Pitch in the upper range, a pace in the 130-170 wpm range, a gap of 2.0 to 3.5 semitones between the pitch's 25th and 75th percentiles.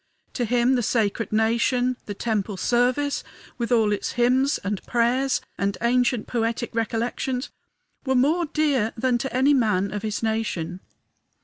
Yes: high, 240 Hz; average, 150 wpm; narrow, 2.6 semitones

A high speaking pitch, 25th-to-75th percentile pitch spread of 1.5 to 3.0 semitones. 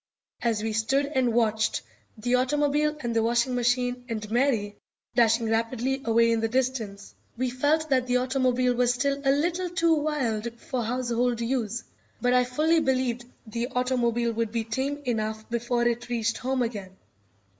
Yes: high, 245 Hz; narrow, 2.4 semitones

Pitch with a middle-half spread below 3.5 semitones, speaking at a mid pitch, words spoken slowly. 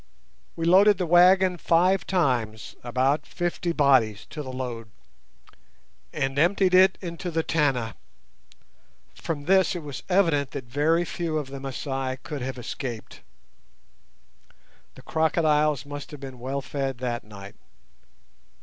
No: average, 4.7 semitones; medium, 145 Hz; slow, 130 wpm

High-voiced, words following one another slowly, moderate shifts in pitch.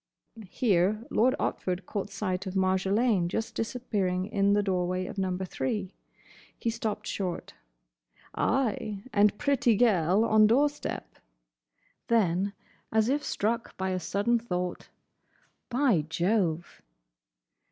Yes: high, 205 Hz; slow, 120 wpm; average, 3.6 semitones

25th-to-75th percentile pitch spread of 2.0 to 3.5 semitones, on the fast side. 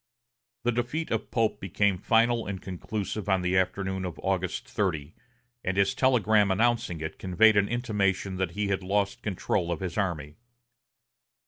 No: average, 2.8 semitones; average, 155 wpm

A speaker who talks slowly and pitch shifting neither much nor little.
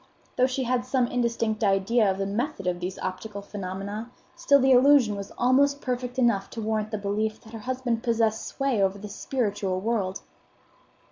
No: average, 180 wpm; average, 3.9 semitones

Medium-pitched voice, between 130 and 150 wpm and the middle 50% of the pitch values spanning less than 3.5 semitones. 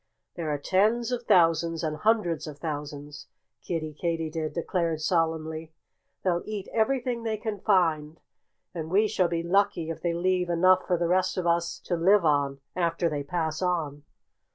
No: medium, 170 Hz; average, 165 wpm; average, 2.9 semitones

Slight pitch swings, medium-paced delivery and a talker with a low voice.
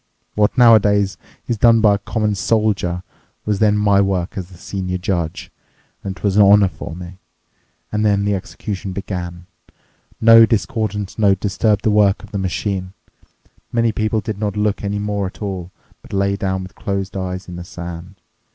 Yes: narrow, 2.2 semitones; average, 180 wpm; low, 100 Hz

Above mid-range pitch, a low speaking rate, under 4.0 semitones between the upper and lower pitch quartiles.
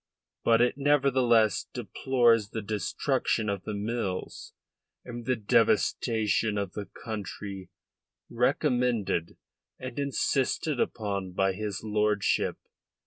No: low, 110 Hz; slow, 100 wpm; average, 3.4 semitones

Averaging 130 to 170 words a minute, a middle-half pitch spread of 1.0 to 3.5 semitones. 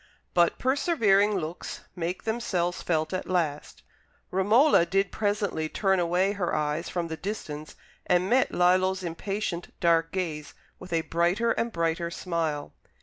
Yes: average, 140 wpm; average, 3.1 semitones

